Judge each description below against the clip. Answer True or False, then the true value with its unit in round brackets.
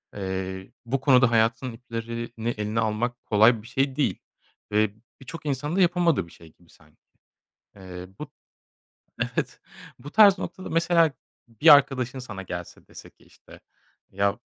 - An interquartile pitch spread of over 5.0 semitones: True (5.4 semitones)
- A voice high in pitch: False (115 Hz)